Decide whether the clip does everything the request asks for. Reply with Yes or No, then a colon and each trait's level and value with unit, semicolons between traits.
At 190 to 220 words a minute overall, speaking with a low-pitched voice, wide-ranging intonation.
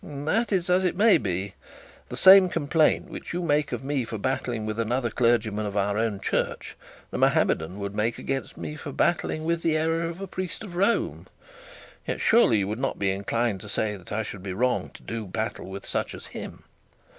Yes: fast, 205 wpm; low, 120 Hz; wide, 8.0 semitones